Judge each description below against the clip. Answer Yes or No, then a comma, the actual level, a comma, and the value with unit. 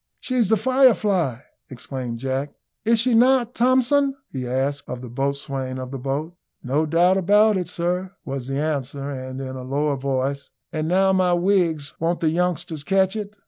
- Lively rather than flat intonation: Yes, wide, 6.1 semitones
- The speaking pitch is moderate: Yes, medium, 155 Hz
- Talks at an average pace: Yes, average, 175 wpm